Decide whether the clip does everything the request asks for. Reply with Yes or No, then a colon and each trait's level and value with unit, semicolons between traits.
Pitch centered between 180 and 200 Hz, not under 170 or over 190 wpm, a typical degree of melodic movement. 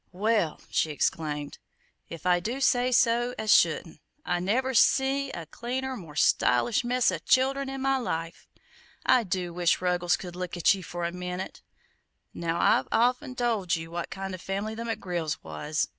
No: high, 190 Hz; average, 180 wpm; wide, 6.2 semitones